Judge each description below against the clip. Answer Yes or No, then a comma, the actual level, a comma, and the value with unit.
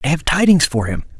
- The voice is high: No, medium, 145 Hz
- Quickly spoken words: Yes, fast, 250 wpm